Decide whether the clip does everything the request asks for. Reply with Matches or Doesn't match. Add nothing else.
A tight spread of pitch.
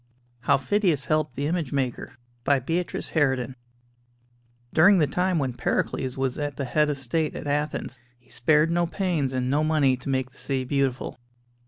Doesn't match